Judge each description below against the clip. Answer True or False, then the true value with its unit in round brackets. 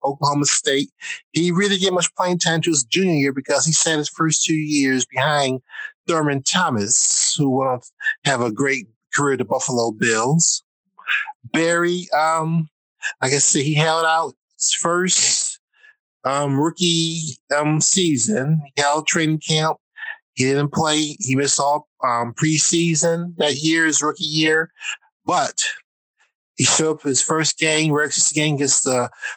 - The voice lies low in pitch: False (155 Hz)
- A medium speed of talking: True (155 wpm)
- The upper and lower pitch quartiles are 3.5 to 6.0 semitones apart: False (3.0 semitones)